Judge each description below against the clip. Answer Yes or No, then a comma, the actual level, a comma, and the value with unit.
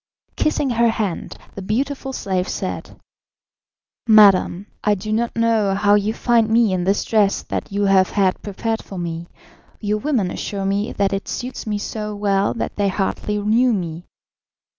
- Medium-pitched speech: No, high, 205 Hz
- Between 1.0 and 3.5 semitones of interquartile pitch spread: Yes, narrow, 2.4 semitones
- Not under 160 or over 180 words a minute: Yes, average, 165 wpm